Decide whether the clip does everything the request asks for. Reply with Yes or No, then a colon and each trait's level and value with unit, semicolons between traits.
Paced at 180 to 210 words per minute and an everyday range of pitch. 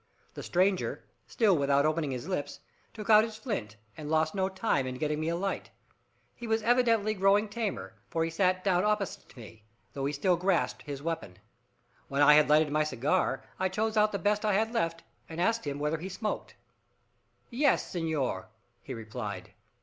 No: average, 190 wpm; wide, 6.0 semitones